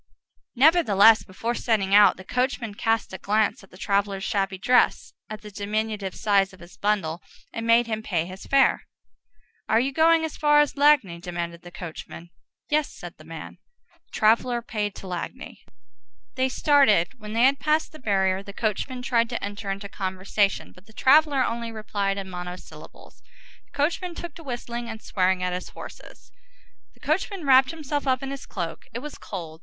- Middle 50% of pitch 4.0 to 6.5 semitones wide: Yes, average, 5.3 semitones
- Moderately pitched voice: No, high, 215 Hz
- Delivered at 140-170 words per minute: No, average, 180 wpm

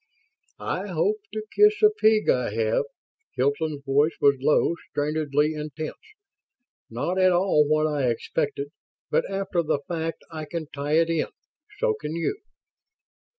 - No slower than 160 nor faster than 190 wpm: No, average, 145 wpm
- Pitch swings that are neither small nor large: Yes, average, 4.3 semitones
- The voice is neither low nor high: Yes, medium, 155 Hz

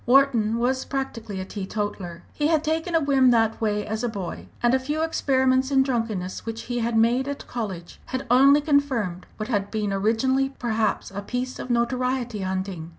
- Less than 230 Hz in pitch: No, high, 235 Hz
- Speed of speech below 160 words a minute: No, average, 185 wpm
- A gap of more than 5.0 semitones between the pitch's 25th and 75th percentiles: No, average, 4.1 semitones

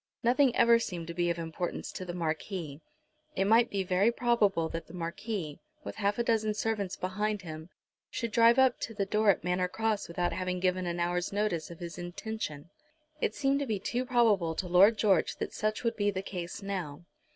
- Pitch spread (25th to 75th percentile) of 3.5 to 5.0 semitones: Yes, average, 4.1 semitones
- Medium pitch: No, high, 195 Hz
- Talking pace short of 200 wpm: No, fast, 205 wpm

